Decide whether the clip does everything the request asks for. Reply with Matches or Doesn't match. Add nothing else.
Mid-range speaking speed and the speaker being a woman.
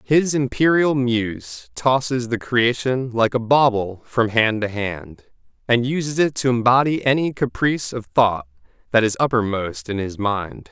Doesn't match